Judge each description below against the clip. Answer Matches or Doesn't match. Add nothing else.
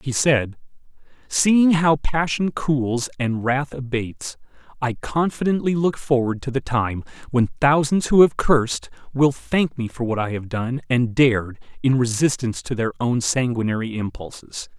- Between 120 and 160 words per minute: Matches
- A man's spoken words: Matches